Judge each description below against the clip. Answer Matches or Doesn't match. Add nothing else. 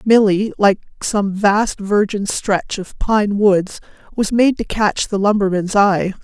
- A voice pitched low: Doesn't match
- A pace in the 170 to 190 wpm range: Doesn't match